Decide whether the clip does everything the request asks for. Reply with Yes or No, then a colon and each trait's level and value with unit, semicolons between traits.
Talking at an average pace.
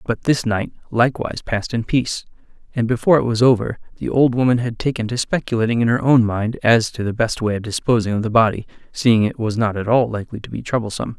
No: fast, 230 wpm